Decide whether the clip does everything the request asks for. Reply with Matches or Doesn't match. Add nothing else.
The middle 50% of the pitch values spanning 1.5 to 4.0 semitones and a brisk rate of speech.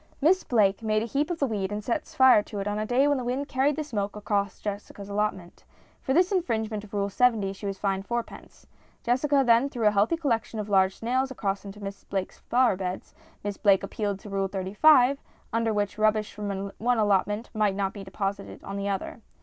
Matches